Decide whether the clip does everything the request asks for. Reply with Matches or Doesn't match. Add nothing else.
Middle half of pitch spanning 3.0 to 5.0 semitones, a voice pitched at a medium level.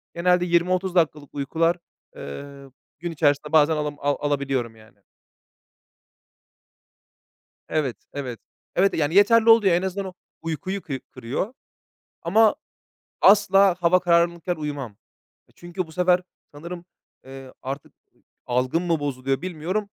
Matches